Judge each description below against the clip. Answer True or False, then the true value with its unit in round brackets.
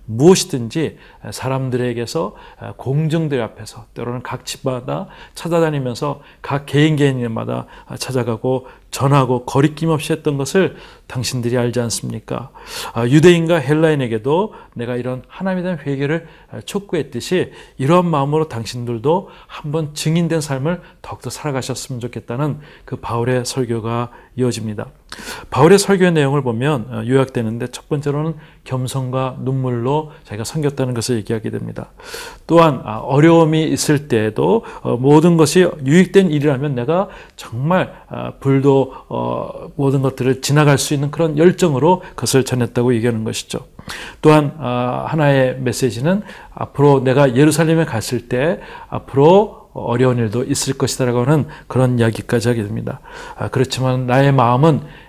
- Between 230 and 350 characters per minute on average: True (320 characters per minute)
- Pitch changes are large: False (4.2 semitones)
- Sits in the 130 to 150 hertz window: True (135 Hz)